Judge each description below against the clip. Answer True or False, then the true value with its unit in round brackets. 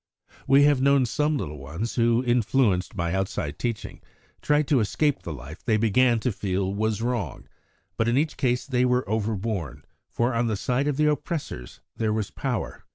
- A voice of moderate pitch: False (115 Hz)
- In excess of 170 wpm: True (185 wpm)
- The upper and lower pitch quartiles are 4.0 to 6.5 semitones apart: True (4.8 semitones)